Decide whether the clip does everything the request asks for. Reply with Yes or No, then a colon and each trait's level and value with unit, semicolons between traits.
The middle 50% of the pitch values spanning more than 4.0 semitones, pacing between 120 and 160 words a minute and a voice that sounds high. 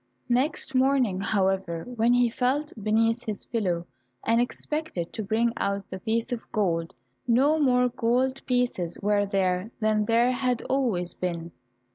Yes: average, 4.4 semitones; average, 145 wpm; high, 230 Hz